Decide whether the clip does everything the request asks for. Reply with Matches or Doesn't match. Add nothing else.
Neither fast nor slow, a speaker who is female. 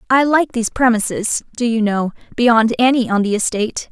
Matches